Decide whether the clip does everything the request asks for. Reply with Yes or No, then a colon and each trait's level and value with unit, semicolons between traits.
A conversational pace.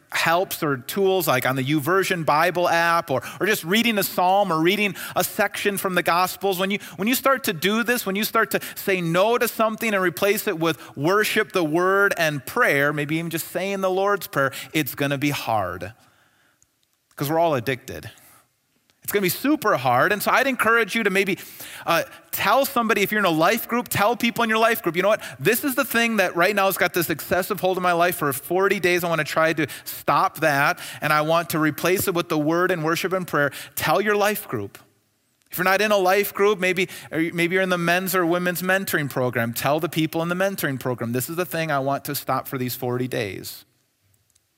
No: fast, 230 wpm